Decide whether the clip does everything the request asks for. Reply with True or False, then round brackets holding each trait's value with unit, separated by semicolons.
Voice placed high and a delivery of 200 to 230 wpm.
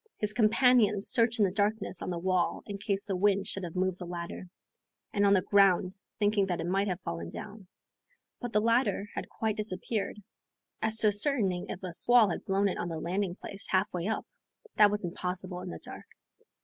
True (200 Hz; 205 wpm)